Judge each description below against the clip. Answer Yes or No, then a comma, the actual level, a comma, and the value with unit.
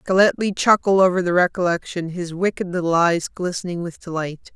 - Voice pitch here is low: No, medium, 180 Hz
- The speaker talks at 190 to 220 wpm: No, average, 160 wpm